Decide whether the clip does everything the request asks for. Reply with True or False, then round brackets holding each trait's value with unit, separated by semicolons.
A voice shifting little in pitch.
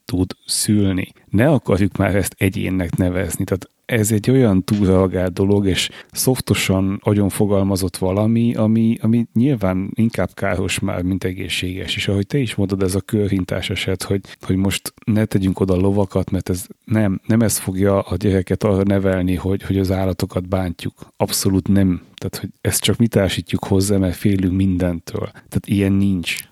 True (1.7 semitones)